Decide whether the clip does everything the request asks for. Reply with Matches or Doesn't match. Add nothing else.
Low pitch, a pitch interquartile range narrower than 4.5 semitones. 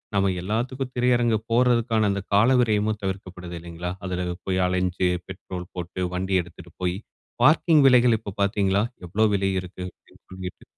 Matches